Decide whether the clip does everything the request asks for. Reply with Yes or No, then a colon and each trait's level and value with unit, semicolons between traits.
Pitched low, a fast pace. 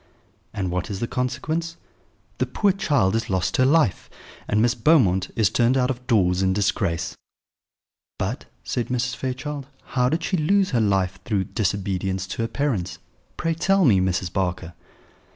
No: low, 115 Hz; average, 165 wpm